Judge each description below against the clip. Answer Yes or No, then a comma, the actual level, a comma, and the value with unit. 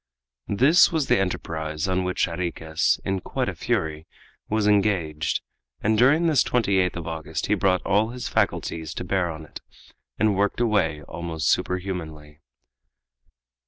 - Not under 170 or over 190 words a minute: No, average, 145 wpm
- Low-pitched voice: Yes, very low, 90 Hz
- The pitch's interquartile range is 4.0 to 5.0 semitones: Yes, average, 4.6 semitones